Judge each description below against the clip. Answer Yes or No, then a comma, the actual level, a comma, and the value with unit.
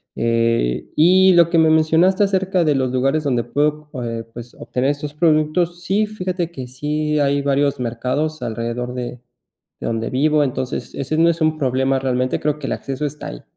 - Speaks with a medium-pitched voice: Yes, medium, 145 Hz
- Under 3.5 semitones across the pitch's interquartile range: No, average, 4.0 semitones